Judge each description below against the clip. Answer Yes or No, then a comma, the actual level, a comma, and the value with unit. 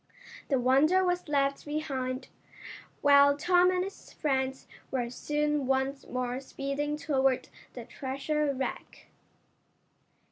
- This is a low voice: No, very high, 275 Hz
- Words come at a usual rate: No, slow, 110 wpm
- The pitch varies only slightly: Yes, narrow, 2.2 semitones